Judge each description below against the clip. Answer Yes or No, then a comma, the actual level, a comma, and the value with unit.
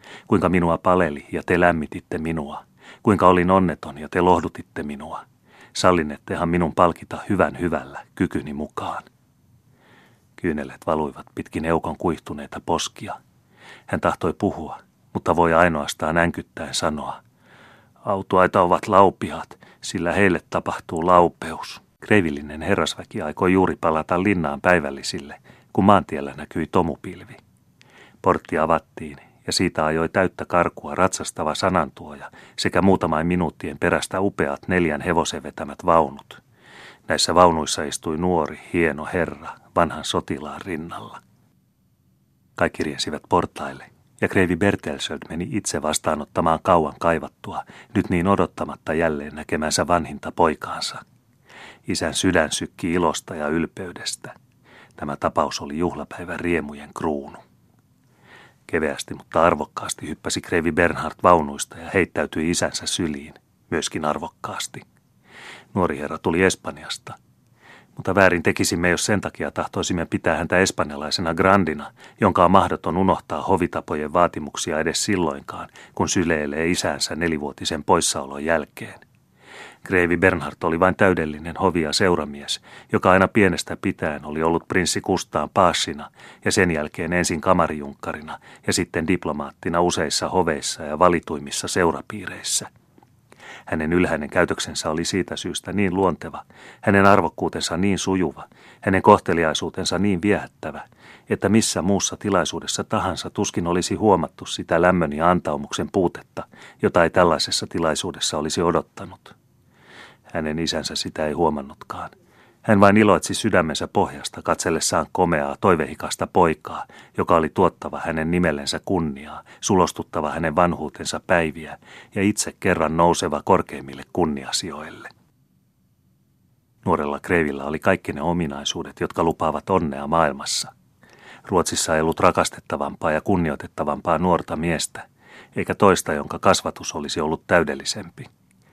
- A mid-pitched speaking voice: No, very low, 85 Hz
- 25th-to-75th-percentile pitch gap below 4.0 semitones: Yes, average, 3.2 semitones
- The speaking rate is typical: Yes, average, 115 wpm